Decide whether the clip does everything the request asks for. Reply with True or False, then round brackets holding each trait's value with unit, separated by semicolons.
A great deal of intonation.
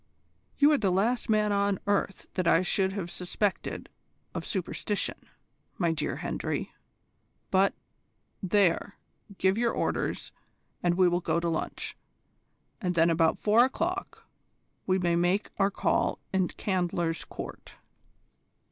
False (2.9 semitones)